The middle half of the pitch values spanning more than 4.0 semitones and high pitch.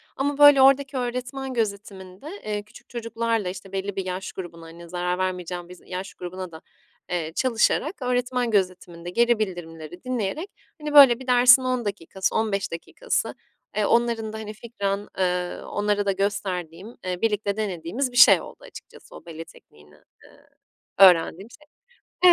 Yes: average, 5.1 semitones; high, 200 Hz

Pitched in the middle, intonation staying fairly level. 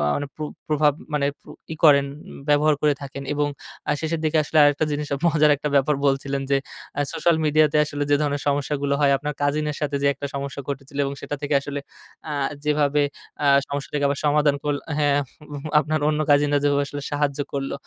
Yes: medium, 145 Hz; narrow, 1.0 semitones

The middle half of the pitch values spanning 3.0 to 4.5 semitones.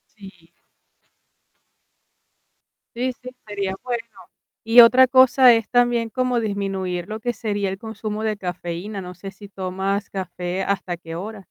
Yes: average, 3.5 semitones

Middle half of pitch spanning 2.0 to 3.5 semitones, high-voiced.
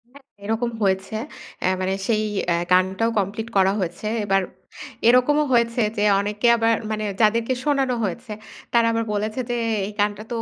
Yes: average, 2.9 semitones; high, 215 Hz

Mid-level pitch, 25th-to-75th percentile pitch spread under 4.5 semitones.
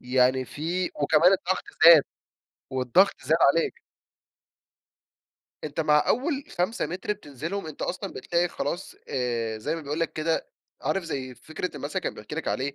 No: medium, 160 Hz; average, 4.9 semitones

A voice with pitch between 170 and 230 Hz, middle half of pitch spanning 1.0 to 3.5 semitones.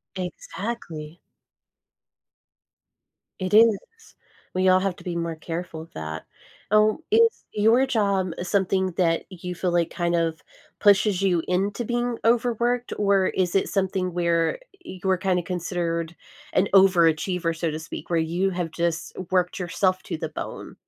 Yes: medium, 185 Hz; average, 2.9 semitones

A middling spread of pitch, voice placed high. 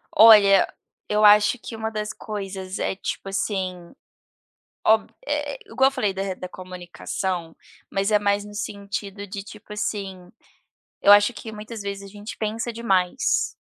No: narrow, 1.9 semitones; high, 205 Hz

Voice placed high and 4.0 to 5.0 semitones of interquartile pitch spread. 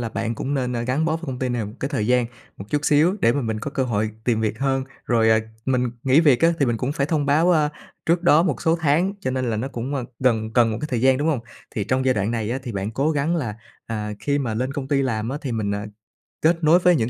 No: low, 130 Hz; average, 4.4 semitones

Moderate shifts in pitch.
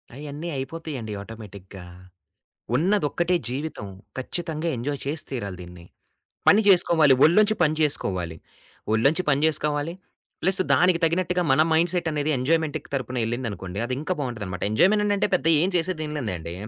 No: wide, 6.3 semitones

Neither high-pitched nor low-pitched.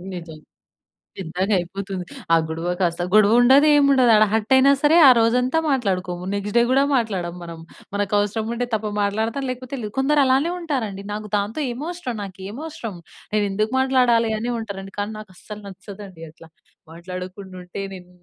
No: high, 210 Hz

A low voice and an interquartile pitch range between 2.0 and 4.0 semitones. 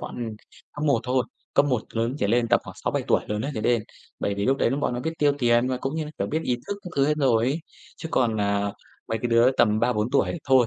Yes: low, 125 Hz; average, 3.6 semitones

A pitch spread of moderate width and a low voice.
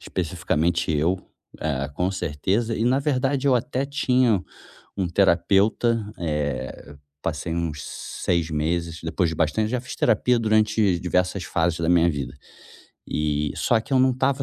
No: wide, 6.1 semitones; very low, 90 Hz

